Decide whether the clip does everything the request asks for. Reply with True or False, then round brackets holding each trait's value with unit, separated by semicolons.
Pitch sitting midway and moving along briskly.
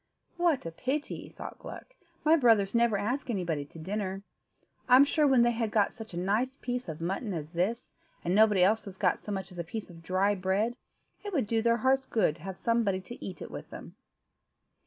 False (210 Hz; 210 wpm)